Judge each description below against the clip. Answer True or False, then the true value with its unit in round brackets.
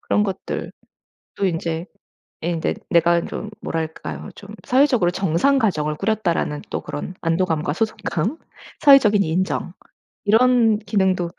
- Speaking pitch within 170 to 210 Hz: True (185 Hz)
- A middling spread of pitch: True (4.8 semitones)